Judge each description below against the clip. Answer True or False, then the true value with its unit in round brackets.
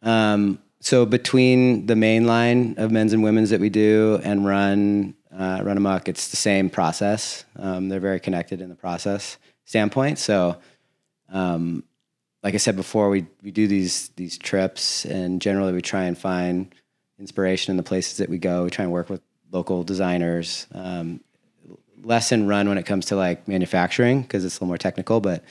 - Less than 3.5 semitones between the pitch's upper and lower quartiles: True (2.8 semitones)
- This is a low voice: True (95 Hz)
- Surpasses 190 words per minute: False (185 wpm)